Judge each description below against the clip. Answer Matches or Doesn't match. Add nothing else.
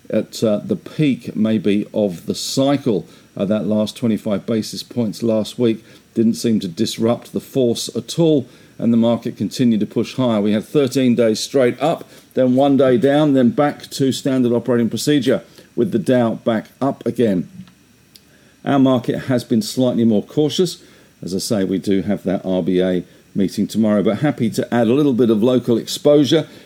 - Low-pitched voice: Matches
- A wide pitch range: Doesn't match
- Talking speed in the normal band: Matches